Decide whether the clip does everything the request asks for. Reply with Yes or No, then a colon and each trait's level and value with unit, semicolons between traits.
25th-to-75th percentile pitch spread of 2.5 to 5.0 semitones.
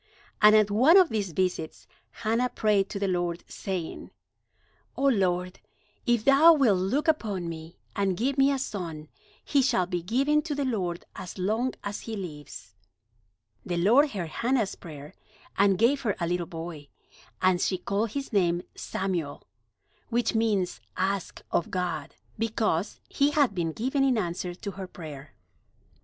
No: wide, 5.4 semitones